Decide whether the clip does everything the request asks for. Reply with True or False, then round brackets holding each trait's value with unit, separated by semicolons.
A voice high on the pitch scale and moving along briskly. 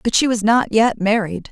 True (215 Hz; 235 wpm)